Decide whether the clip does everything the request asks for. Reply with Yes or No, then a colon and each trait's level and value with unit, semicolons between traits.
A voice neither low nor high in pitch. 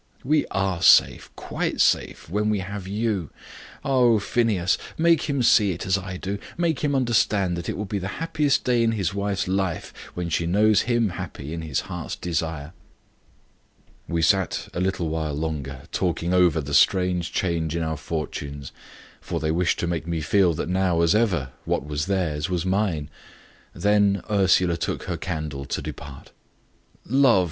No: very low, 90 Hz